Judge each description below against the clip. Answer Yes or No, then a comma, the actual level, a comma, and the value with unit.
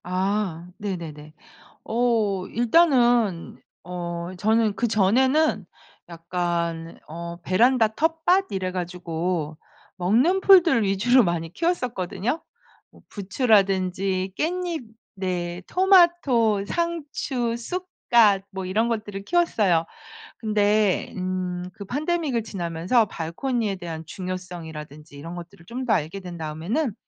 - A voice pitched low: No, high, 200 Hz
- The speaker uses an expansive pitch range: Yes, wide, 5.8 semitones